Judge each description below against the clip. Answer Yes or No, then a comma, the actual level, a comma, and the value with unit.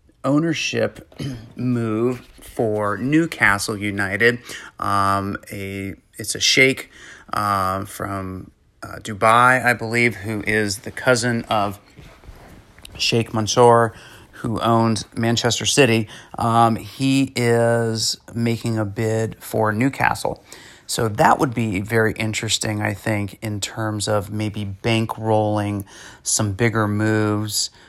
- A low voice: Yes, low, 110 Hz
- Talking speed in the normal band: No, slow, 110 wpm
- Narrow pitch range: Yes, narrow, 2.0 semitones